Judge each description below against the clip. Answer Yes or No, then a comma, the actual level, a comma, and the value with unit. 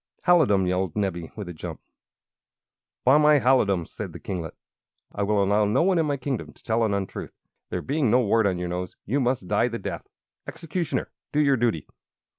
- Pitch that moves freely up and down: Yes, wide, 6.3 semitones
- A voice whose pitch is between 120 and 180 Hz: No, low, 110 Hz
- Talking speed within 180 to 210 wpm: Yes, average, 195 wpm